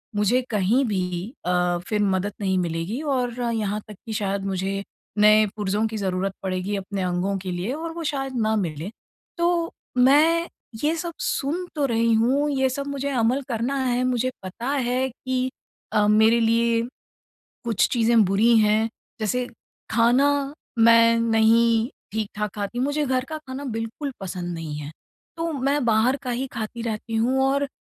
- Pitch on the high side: Yes, high, 230 Hz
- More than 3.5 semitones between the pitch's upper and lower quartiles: Yes, average, 4.4 semitones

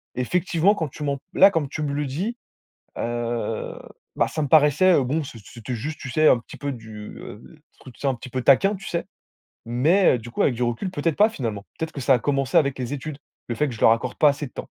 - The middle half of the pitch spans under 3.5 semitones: No, average, 4.6 semitones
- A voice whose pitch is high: No, medium, 140 Hz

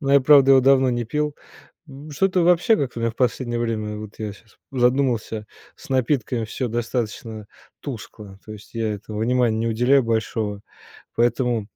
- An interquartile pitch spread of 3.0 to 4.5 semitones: Yes, average, 3.4 semitones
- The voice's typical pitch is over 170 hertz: No, low, 120 Hz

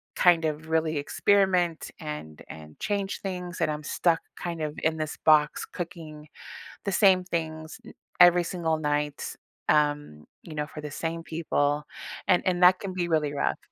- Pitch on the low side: No, medium, 160 Hz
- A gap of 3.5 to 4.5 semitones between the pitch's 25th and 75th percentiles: No, average, 2.8 semitones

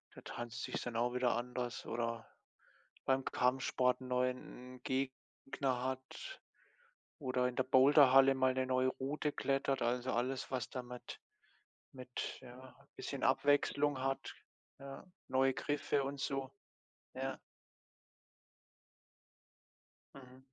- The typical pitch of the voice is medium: No, low, 130 Hz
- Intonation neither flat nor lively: No, narrow, 1.2 semitones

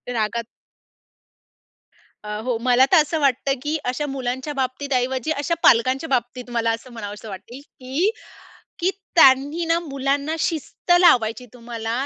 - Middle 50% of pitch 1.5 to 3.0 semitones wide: No, average, 3.8 semitones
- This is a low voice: No, very high, 260 Hz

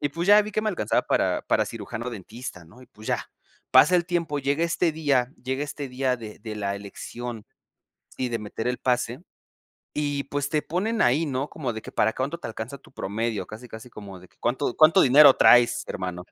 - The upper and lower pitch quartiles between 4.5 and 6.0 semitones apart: Yes, average, 4.8 semitones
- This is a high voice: No, low, 125 Hz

